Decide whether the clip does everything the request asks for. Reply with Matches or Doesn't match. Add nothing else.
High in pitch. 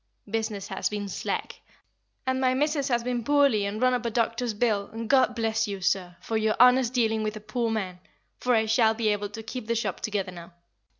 Matches